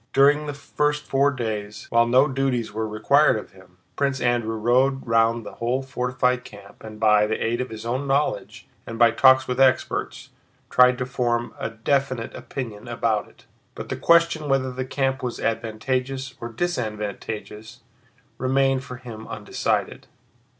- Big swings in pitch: No, average, 3.1 semitones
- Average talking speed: Yes, average, 160 wpm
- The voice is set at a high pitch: No, low, 125 Hz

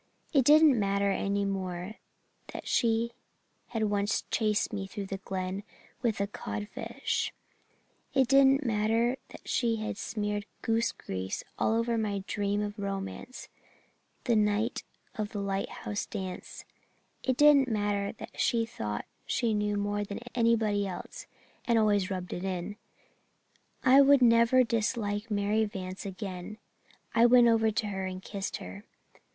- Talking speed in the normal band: Yes, average, 145 wpm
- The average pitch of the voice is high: Yes, high, 210 Hz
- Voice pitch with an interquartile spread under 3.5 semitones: Yes, narrow, 2.6 semitones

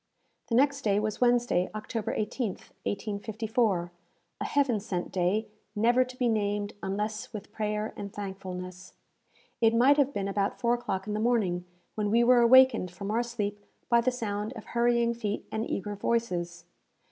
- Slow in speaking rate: No, average, 165 wpm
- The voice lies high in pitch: Yes, high, 215 Hz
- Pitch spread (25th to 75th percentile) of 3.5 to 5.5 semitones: No, average, 2.9 semitones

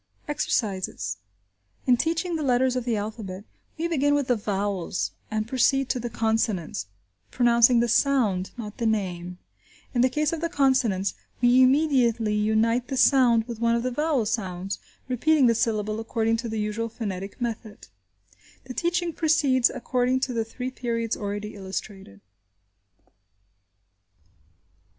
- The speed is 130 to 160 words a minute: Yes, average, 145 wpm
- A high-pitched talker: Yes, high, 235 Hz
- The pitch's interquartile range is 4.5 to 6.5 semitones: No, average, 3.6 semitones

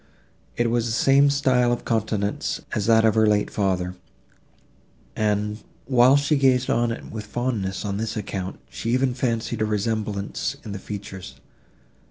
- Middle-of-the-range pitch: No, low, 110 Hz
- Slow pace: No, average, 160 wpm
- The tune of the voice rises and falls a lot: No, average, 3.0 semitones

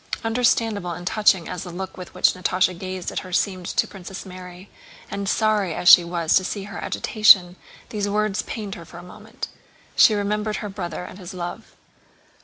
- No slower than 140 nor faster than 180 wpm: No, average, 190 wpm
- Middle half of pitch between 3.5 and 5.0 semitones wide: No, average, 2.7 semitones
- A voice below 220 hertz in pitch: Yes, high, 190 Hz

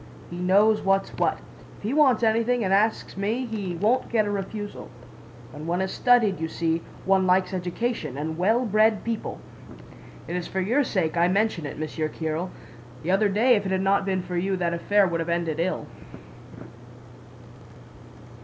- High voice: Yes, high, 195 Hz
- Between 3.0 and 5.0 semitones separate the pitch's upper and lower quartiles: Yes, average, 4.0 semitones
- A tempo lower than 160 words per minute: No, average, 180 wpm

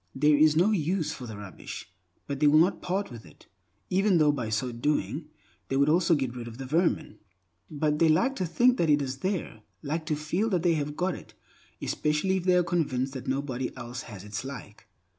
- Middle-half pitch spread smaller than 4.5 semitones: No, average, 5.0 semitones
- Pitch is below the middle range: No, medium, 150 Hz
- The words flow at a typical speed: No, fast, 215 wpm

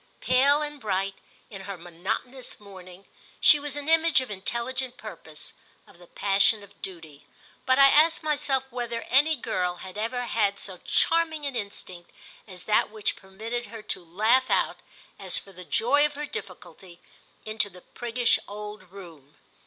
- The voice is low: No, high, 215 Hz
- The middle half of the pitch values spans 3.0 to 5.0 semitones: No, wide, 5.6 semitones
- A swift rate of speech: No, average, 160 wpm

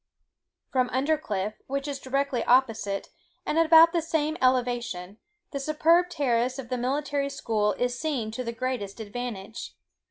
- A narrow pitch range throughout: No, average, 3.8 semitones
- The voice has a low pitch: No, very high, 255 Hz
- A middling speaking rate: Yes, average, 150 wpm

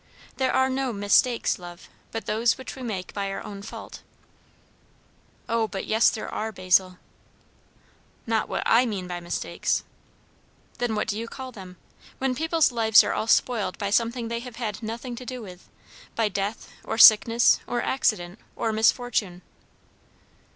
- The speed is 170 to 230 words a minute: No, average, 160 wpm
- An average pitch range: Yes, average, 3.4 semitones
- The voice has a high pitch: Yes, high, 225 Hz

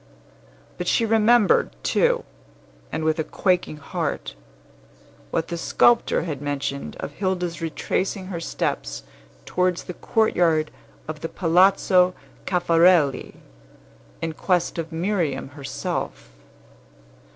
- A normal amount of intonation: Yes, average, 3.1 semitones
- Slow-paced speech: Yes, slow, 105 wpm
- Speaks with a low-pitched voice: No, medium, 170 Hz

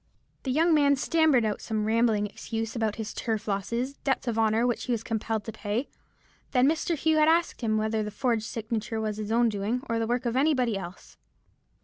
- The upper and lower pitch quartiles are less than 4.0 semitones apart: Yes, average, 3.1 semitones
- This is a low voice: No, high, 230 Hz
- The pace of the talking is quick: Yes, fast, 210 wpm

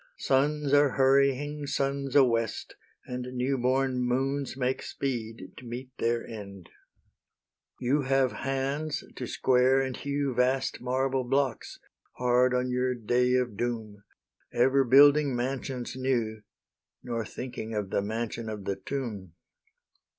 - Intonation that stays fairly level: Yes, narrow, 2.3 semitones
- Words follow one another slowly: Yes, slow, 130 wpm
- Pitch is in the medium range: No, low, 125 Hz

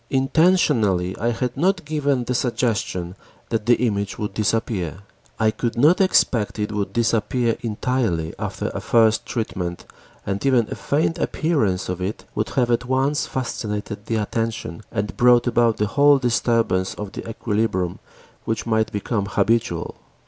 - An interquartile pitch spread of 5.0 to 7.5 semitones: No, average, 3.3 semitones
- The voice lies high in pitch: No, low, 115 Hz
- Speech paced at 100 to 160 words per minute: Yes, average, 150 wpm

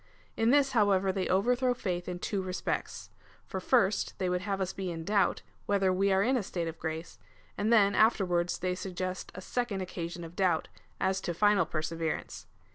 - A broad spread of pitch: No, narrow, 2.5 semitones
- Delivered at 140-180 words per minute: No, average, 195 wpm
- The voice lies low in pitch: No, high, 190 Hz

